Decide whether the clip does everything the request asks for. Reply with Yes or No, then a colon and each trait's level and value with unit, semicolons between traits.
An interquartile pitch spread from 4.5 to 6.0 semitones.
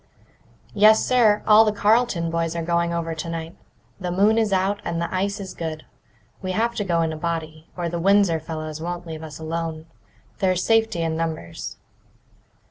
No: average, 3.7 semitones